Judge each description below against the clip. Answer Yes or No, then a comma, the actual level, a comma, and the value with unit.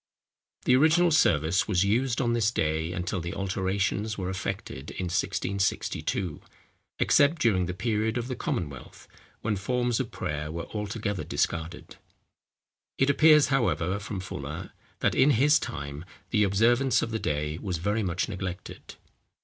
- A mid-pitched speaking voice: No, low, 100 Hz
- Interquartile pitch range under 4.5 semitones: No, average, 5.3 semitones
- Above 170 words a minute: No, average, 145 wpm